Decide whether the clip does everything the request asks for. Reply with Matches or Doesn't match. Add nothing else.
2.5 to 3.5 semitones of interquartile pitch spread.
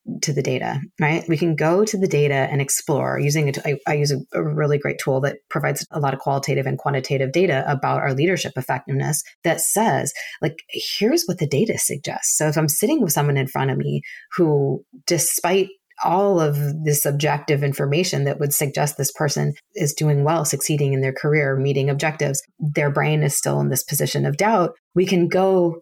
Matches